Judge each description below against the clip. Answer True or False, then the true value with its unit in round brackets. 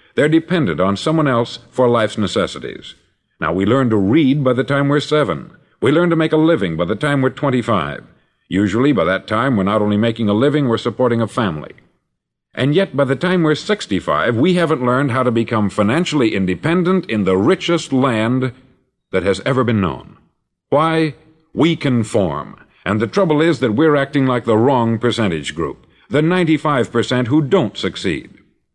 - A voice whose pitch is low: True (130 Hz)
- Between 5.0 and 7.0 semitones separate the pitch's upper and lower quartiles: True (5.6 semitones)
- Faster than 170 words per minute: True (180 wpm)